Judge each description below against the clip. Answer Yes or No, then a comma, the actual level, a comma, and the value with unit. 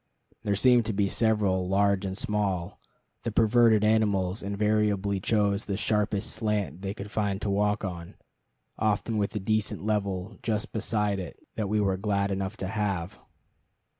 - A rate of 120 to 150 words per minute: No, average, 165 wpm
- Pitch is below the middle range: Yes, low, 105 Hz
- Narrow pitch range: Yes, narrow, 1.7 semitones